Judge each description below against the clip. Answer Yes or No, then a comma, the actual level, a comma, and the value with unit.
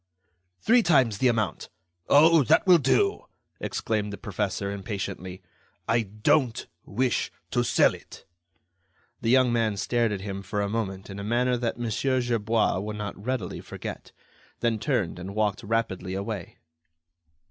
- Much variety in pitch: No, average, 3.4 semitones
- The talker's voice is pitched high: No, low, 110 Hz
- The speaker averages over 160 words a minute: No, average, 145 wpm